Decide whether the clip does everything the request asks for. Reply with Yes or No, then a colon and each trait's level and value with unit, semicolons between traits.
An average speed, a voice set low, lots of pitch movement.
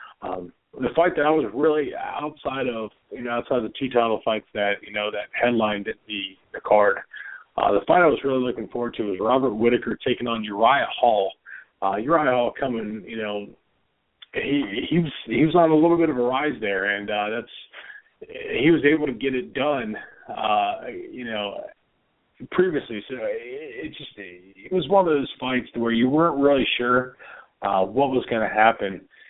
Yes: average, 195 wpm; low, 125 Hz; wide, 6.1 semitones